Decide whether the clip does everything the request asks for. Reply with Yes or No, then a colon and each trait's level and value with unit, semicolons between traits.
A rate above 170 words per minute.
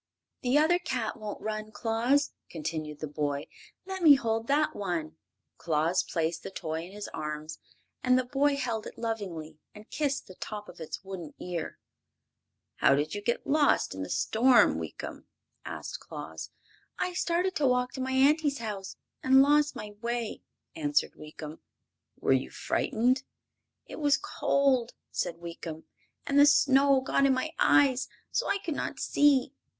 No: average, 160 wpm